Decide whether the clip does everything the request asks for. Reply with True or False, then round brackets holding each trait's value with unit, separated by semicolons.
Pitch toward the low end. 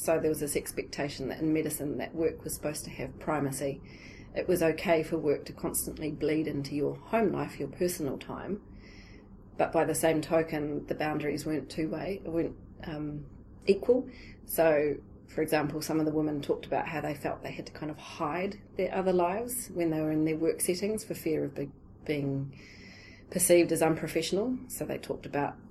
False (155 Hz)